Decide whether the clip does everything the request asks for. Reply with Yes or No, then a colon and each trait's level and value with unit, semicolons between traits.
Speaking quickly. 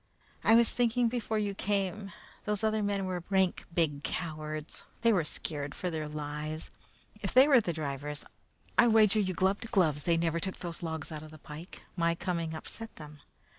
No: average, 190 wpm